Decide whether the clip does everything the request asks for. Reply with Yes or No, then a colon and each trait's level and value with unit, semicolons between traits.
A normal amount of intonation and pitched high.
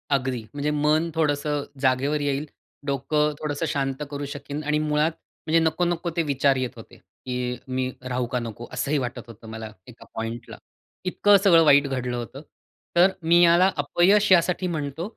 No: average, 3.9 semitones; medium, 145 Hz